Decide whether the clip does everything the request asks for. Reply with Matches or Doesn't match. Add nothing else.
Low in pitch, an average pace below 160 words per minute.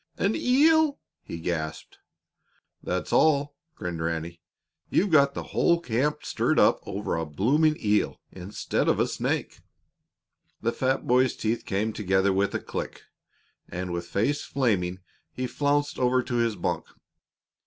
Matches